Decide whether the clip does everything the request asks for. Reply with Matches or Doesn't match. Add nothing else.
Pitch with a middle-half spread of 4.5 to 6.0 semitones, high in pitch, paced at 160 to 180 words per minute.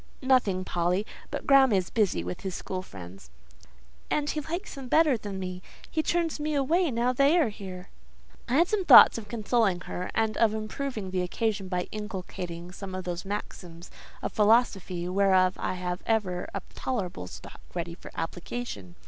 Matches